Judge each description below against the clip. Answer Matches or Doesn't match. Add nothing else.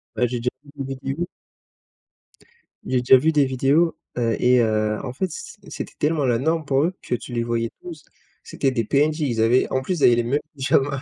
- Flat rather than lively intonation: Doesn't match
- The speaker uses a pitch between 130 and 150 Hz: Matches